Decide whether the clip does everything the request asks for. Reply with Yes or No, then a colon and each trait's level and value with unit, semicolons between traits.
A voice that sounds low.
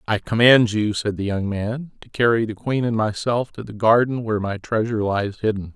Yes: low, 110 Hz